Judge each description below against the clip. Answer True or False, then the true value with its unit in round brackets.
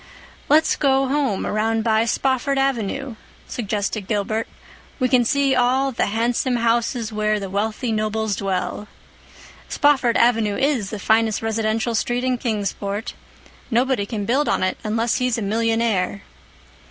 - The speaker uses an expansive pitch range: False (3.0 semitones)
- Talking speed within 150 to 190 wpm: False (140 wpm)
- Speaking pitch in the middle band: False (225 Hz)